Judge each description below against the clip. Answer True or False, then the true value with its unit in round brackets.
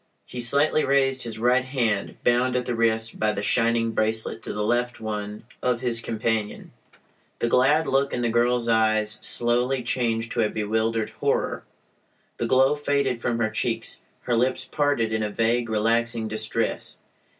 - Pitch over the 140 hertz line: False (115 Hz)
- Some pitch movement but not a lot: False (2.1 semitones)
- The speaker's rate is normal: True (165 wpm)